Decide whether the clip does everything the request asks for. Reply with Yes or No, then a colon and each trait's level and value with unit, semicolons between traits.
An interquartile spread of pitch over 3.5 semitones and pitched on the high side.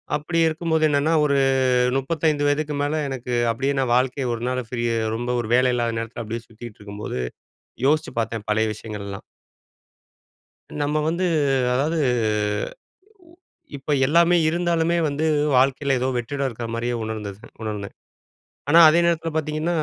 No: average, 5.1 semitones; low, 135 Hz